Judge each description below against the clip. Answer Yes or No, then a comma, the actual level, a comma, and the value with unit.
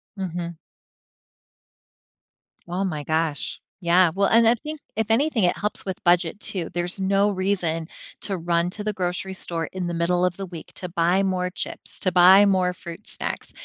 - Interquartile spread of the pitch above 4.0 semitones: No, narrow, 2.4 semitones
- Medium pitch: Yes, medium, 180 Hz